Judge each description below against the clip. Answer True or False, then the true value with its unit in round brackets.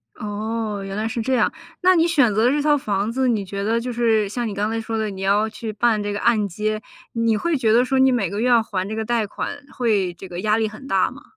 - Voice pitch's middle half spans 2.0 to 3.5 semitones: True (2.7 semitones)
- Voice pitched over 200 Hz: True (220 Hz)